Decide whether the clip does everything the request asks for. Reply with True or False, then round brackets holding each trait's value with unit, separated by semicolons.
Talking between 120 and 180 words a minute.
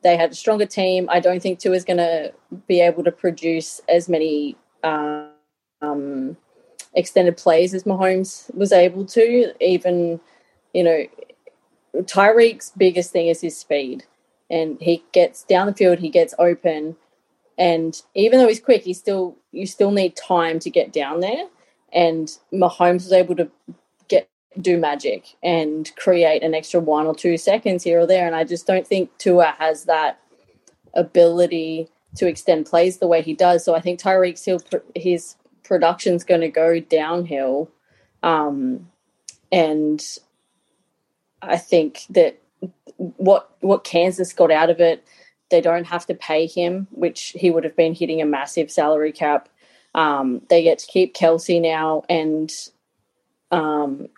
True (155 wpm)